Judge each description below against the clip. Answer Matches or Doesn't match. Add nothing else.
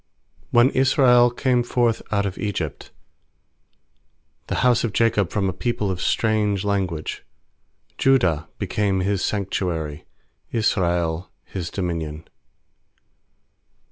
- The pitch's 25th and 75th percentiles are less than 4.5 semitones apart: Doesn't match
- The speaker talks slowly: Matches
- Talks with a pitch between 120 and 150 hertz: Doesn't match